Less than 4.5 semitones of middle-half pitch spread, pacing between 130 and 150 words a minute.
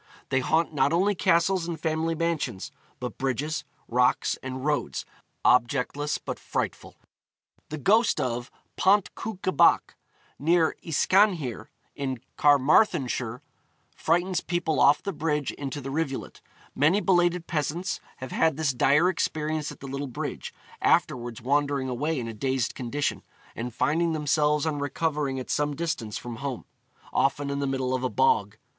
Yes: average, 3.9 semitones; average, 145 wpm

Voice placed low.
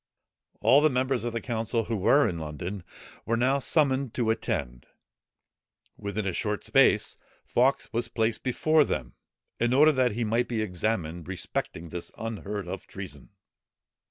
Yes: low, 115 Hz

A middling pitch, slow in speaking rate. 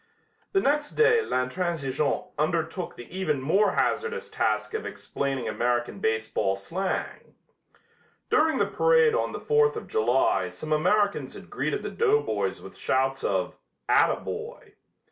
Yes: medium, 165 Hz; slow, 130 wpm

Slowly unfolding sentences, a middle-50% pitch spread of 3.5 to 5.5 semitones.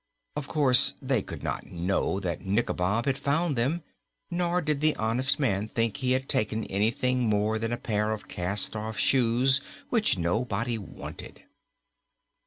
No: average, 155 wpm; average, 4.4 semitones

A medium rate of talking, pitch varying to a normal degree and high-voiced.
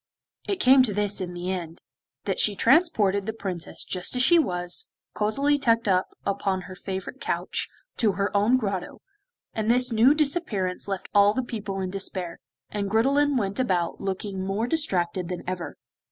Yes: average, 170 wpm; average, 4.9 semitones; high, 200 Hz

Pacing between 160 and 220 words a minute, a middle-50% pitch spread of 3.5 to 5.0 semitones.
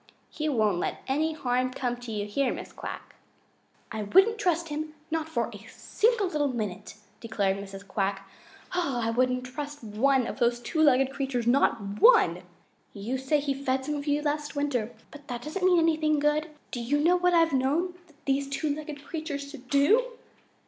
Yes: average, 180 wpm; average, 4.2 semitones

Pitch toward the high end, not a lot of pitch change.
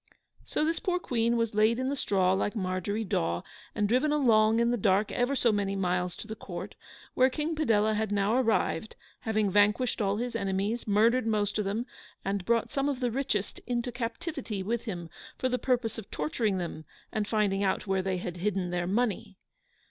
No: high, 215 Hz; average, 3.7 semitones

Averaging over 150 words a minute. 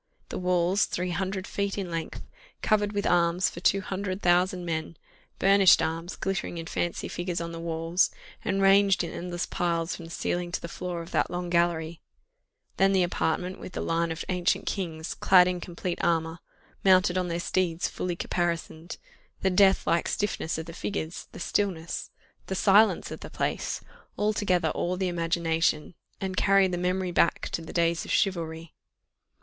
Yes: average, 175 wpm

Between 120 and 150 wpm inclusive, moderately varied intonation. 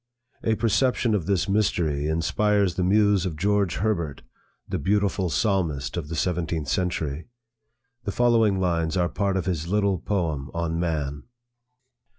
Yes: average, 145 wpm; average, 4.0 semitones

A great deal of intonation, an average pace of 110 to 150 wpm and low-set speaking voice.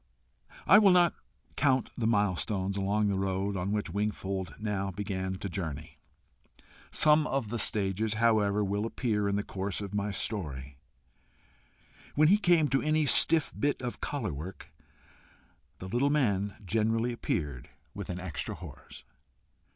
No: average, 4.1 semitones; average, 145 wpm; low, 105 Hz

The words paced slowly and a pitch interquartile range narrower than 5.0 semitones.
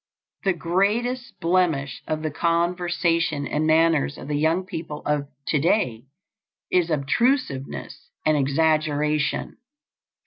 Yes: slow, 110 wpm; average, 3.1 semitones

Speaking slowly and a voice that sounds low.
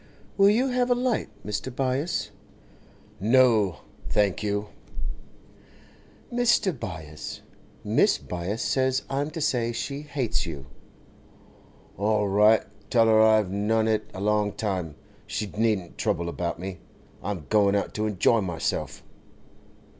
Yes: slow, 125 wpm; low, 110 Hz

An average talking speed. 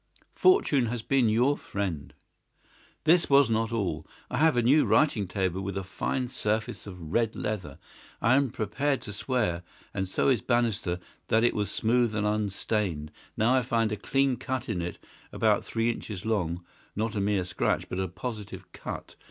Yes: average, 175 wpm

